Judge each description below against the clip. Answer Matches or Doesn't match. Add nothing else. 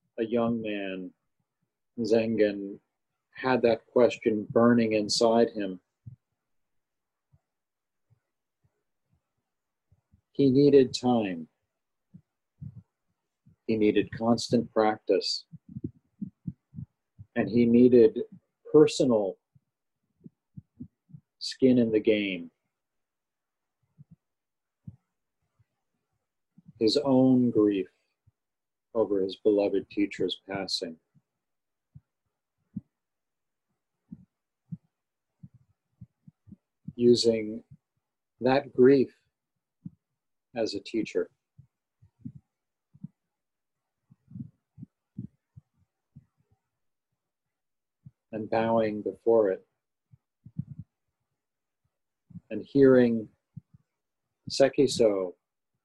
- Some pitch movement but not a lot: Matches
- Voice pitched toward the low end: Matches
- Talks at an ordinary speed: Doesn't match